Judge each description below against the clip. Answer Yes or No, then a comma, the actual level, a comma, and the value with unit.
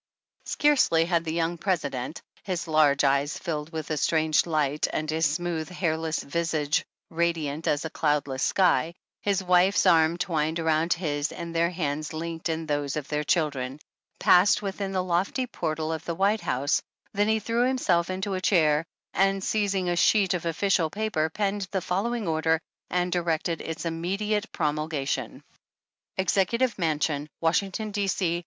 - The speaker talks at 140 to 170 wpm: Yes, average, 165 wpm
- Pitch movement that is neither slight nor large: Yes, average, 3.4 semitones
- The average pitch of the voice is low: No, medium, 165 Hz